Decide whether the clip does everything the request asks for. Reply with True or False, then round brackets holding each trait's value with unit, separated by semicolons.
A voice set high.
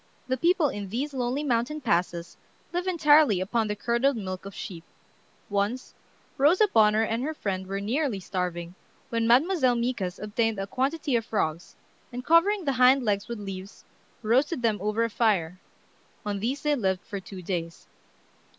True (230 Hz)